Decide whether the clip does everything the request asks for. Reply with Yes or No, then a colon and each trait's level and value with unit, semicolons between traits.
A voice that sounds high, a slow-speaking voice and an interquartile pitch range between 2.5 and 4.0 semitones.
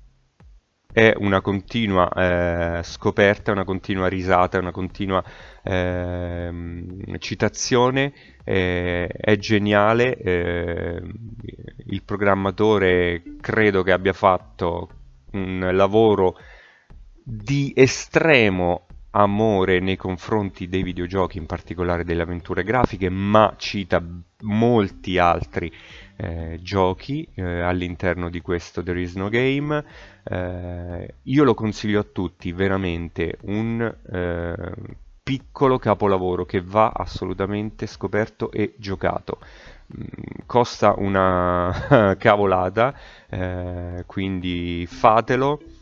No: very low, 95 Hz; slow, 95 wpm; average, 3.4 semitones